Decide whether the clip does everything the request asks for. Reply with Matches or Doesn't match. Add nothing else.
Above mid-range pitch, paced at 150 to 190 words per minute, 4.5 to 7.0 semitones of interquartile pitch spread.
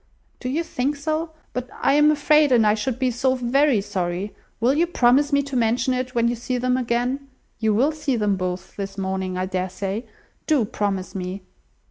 Doesn't match